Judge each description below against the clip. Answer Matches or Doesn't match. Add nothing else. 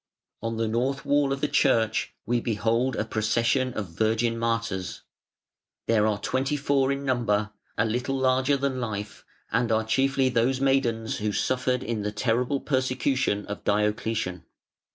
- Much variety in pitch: Doesn't match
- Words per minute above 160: Doesn't match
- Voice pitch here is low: Matches